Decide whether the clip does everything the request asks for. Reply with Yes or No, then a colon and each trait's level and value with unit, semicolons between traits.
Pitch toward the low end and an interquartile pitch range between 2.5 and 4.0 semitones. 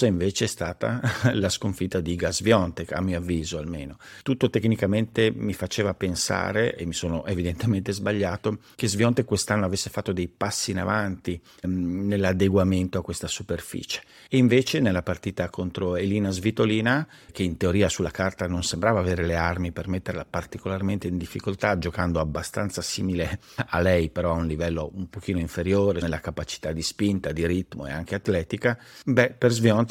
Yes: very low, 95 Hz; average, 3.4 semitones